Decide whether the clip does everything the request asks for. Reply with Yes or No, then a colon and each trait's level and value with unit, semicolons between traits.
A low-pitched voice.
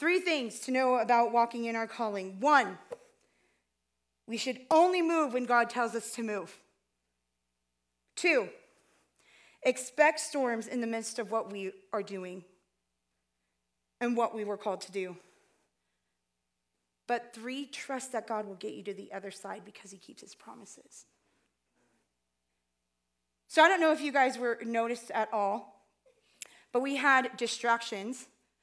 No: high, 220 Hz